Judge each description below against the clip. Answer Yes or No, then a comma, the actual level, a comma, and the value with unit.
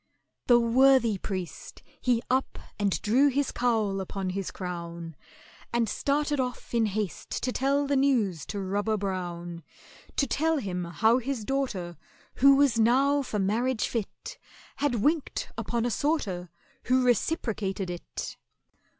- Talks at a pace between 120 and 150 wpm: Yes, average, 140 wpm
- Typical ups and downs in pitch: No, wide, 5.7 semitones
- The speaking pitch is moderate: No, high, 230 Hz